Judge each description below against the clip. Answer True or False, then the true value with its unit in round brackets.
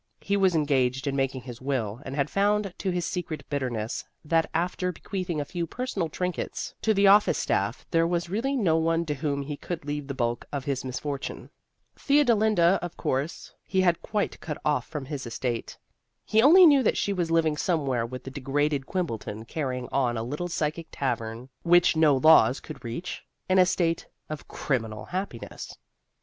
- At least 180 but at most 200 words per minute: True (185 wpm)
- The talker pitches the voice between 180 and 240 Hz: False (155 Hz)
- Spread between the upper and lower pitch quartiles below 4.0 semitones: False (5.3 semitones)